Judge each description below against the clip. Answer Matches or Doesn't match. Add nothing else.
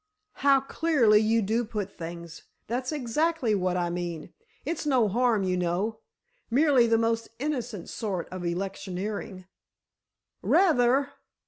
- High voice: Matches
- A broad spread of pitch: Matches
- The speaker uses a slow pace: Matches